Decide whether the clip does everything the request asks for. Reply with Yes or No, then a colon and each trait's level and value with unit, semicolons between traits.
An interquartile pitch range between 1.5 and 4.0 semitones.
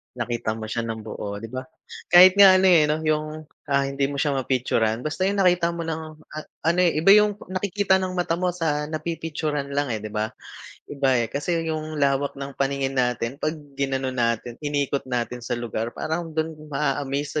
No: average, 4.4 semitones